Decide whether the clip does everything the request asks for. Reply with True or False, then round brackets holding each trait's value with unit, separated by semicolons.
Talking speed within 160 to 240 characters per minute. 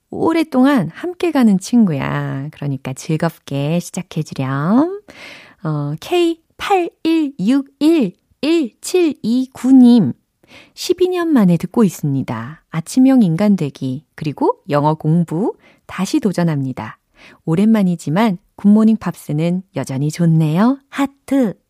True (210 characters per minute)